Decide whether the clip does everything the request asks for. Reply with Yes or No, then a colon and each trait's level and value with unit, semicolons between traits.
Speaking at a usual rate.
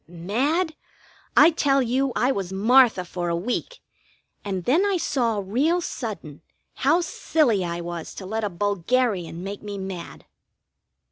Yes: average, 145 wpm